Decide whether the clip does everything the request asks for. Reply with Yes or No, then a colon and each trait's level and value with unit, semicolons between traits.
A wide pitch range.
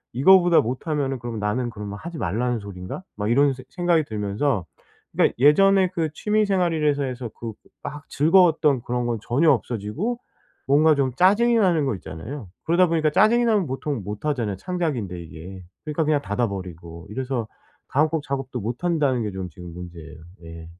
Yes: wide, 7.5 semitones